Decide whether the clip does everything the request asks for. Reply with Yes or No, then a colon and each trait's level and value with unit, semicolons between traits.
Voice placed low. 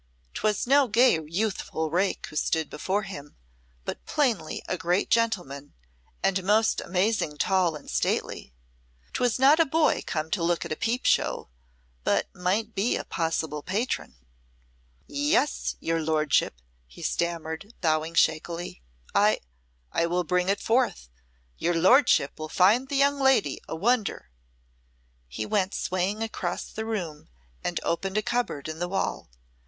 No: medium, 185 Hz